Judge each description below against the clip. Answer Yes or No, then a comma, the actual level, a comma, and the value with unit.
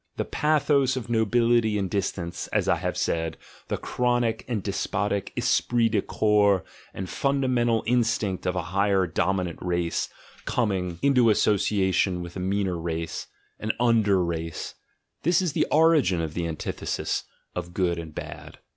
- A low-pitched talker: Yes, low, 100 Hz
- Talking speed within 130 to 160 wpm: Yes, average, 145 wpm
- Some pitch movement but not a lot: Yes, average, 5.0 semitones